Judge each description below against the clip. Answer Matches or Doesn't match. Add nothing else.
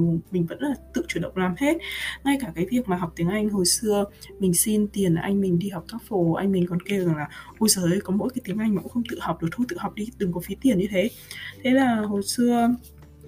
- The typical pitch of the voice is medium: Doesn't match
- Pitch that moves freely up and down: Doesn't match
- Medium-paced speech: Doesn't match